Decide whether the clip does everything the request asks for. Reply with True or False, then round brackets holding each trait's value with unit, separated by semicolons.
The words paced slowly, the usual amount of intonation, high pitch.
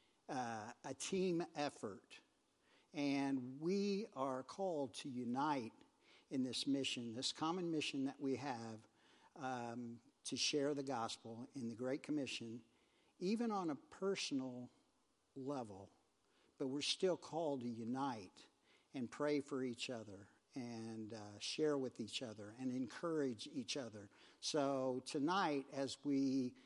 False (130 wpm; 3.3 semitones; 135 Hz)